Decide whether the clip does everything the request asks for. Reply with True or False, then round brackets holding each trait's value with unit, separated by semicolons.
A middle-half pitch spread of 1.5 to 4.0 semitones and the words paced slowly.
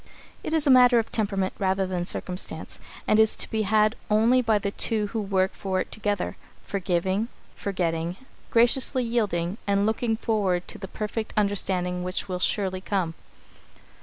False (2.9 semitones; 165 wpm)